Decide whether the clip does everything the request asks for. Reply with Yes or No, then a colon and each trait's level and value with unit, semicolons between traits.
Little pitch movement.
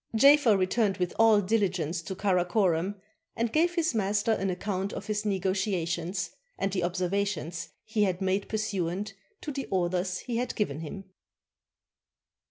No: average, 3.0 semitones